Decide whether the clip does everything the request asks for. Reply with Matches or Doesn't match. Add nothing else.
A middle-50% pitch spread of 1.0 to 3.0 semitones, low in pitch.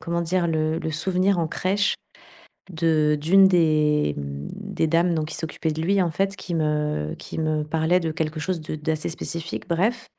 Doesn't match